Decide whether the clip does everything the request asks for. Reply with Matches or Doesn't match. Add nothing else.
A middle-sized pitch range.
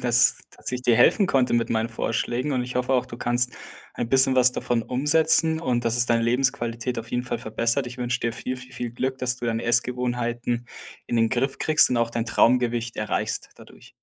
Doesn't match